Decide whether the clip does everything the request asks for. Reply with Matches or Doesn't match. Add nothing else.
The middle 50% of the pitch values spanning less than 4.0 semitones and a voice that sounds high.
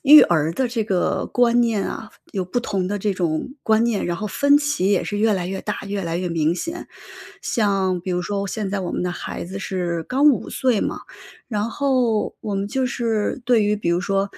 Doesn't match